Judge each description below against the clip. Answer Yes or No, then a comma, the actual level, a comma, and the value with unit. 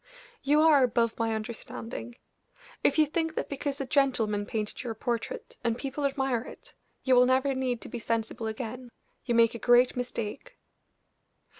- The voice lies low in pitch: No, high, 245 Hz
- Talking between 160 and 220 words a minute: Yes, average, 165 wpm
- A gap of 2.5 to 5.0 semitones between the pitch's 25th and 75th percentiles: Yes, average, 3.1 semitones